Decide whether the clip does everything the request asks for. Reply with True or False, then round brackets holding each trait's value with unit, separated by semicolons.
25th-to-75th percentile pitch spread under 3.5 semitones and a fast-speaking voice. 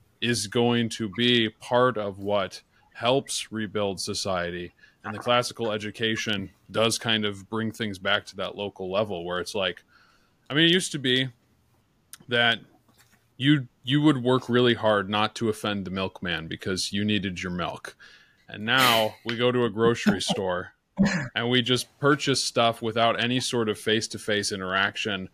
False (2.9 semitones; 170 wpm)